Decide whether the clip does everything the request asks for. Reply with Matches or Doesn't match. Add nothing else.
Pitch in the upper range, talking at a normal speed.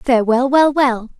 Matches